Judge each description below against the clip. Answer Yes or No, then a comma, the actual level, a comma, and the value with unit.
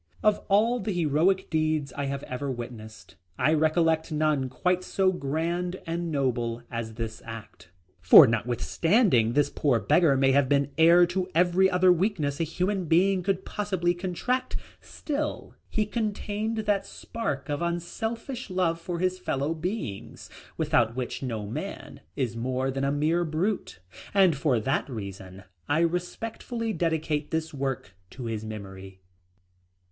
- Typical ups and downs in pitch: No, wide, 6.0 semitones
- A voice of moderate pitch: Yes, medium, 160 Hz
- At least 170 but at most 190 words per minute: No, average, 145 wpm